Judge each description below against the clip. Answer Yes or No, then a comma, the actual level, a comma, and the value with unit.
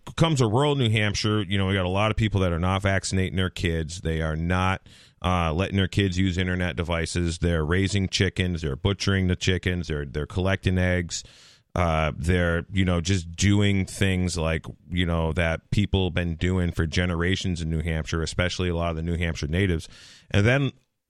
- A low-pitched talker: Yes, very low, 90 Hz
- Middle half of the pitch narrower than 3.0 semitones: Yes, narrow, 2.6 semitones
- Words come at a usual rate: Yes, average, 195 wpm